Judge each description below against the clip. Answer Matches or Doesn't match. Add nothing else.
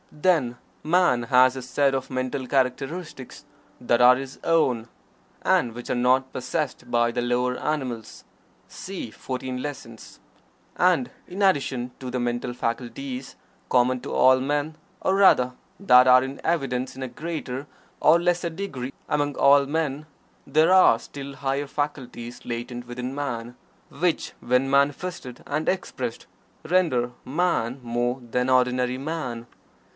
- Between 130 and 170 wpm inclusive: Matches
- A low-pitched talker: Matches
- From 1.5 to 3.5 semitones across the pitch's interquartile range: Matches